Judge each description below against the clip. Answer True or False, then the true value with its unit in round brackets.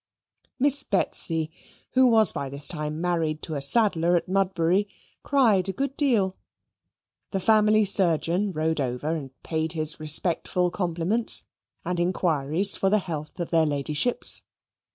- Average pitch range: True (4.4 semitones)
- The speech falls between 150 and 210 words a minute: False (140 wpm)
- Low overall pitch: False (175 Hz)